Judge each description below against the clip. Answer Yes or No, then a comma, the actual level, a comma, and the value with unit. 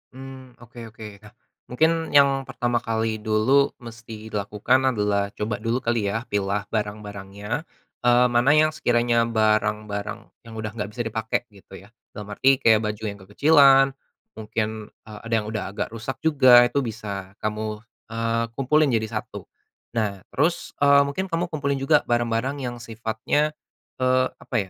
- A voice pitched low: Yes, low, 115 Hz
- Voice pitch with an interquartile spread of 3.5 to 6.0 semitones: Yes, average, 3.8 semitones